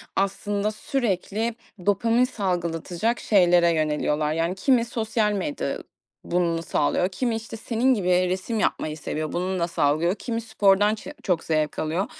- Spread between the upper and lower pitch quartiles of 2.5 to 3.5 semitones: No, average, 4.7 semitones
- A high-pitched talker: Yes, high, 195 Hz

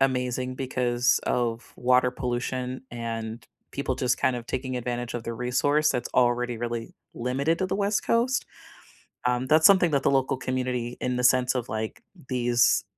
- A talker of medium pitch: No, low, 125 Hz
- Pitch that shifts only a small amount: Yes, narrow, 1.4 semitones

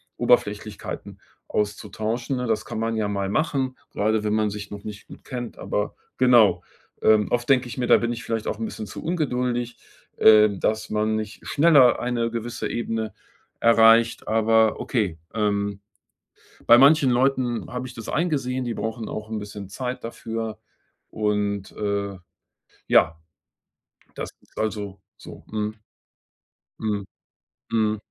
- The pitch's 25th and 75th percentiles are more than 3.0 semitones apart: No, narrow, 2.6 semitones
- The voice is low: Yes, low, 110 Hz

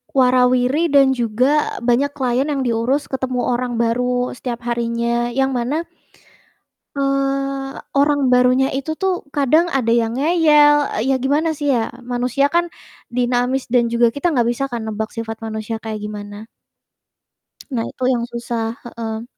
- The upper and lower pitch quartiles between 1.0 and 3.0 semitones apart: Yes, average, 2.7 semitones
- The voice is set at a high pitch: Yes, very high, 250 Hz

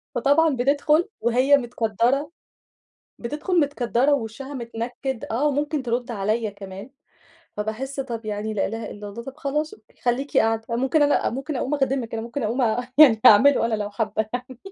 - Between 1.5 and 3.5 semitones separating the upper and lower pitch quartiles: No, average, 3.9 semitones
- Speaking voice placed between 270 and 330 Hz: No, high, 245 Hz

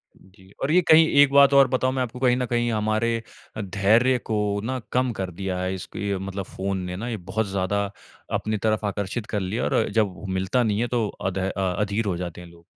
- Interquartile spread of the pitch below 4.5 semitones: Yes, average, 4.1 semitones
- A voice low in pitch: Yes, low, 105 Hz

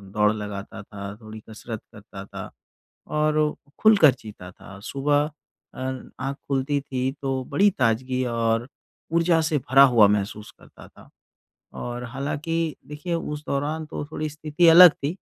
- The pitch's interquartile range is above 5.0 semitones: Yes, wide, 5.6 semitones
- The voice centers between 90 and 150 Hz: Yes, low, 135 Hz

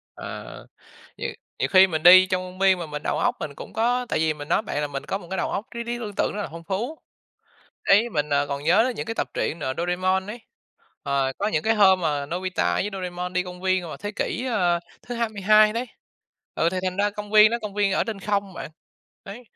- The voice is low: No, high, 190 Hz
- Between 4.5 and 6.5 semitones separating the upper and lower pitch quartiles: No, average, 3.8 semitones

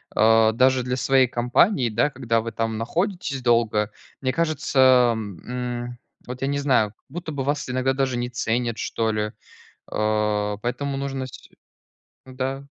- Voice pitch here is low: Yes, low, 125 Hz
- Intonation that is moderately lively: Yes, average, 3.0 semitones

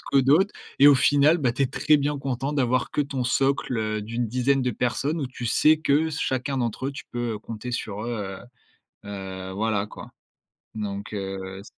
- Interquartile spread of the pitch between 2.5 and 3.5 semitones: No, average, 4.5 semitones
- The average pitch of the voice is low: Yes, low, 125 Hz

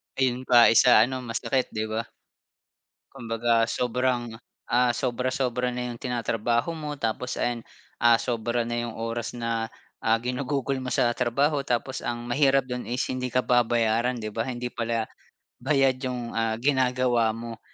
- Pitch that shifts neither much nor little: No, narrow, 1.6 semitones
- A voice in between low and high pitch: No, low, 120 Hz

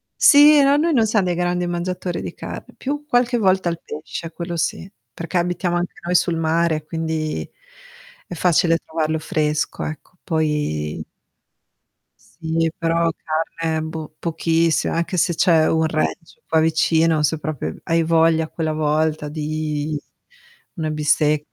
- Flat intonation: Yes, narrow, 2.0 semitones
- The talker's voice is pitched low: No, medium, 165 Hz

